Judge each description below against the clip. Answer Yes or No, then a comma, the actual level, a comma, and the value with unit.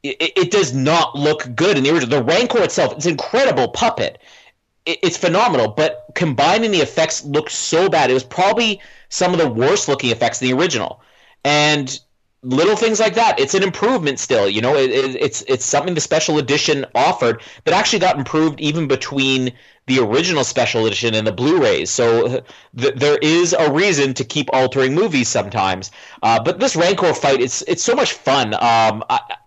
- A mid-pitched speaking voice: Yes, medium, 150 Hz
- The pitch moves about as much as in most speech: No, wide, 6.3 semitones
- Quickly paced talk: No, average, 190 wpm